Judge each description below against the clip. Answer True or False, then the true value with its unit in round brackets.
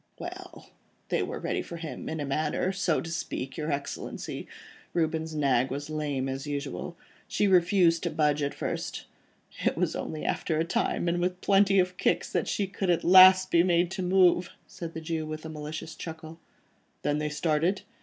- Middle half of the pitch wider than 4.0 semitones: False (3.0 semitones)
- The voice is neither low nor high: True (160 Hz)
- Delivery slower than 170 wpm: False (180 wpm)